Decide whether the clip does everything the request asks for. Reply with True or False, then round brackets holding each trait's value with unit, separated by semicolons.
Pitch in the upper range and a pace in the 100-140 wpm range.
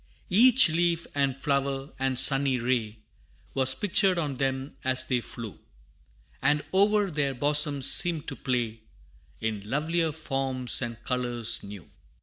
False (135 Hz; 135 wpm)